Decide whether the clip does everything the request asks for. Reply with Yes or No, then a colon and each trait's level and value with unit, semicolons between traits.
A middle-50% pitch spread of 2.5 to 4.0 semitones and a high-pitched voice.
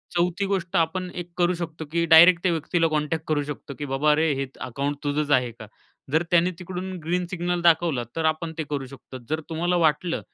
No: average, 2.9 semitones; medium, 160 Hz